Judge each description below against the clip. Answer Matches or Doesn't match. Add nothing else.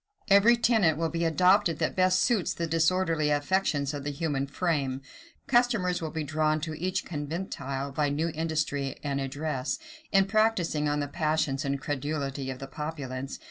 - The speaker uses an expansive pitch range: Doesn't match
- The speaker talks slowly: Doesn't match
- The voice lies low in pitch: Doesn't match